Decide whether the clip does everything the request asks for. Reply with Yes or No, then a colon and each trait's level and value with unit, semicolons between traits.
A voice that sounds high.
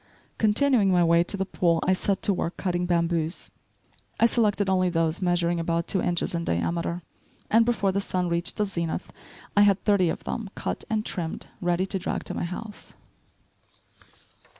No: medium, 180 Hz